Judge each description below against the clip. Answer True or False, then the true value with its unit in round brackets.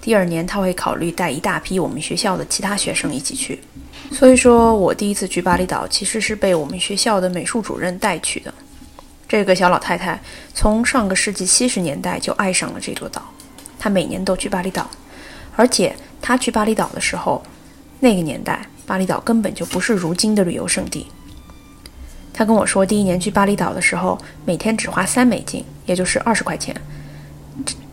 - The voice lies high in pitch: True (195 Hz)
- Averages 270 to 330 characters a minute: True (295 characters per minute)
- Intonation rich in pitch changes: False (3.7 semitones)